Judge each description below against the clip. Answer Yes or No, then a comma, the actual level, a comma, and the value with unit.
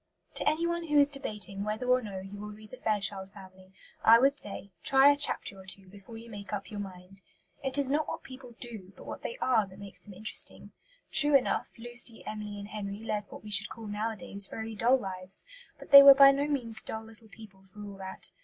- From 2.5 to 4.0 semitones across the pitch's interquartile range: No, average, 4.4 semitones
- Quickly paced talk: Yes, fast, 225 wpm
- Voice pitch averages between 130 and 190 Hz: No, high, 215 Hz